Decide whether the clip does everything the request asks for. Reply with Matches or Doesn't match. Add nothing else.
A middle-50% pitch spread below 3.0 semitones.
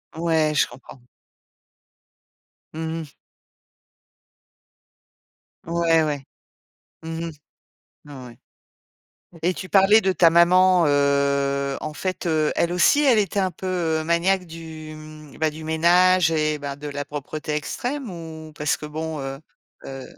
Matches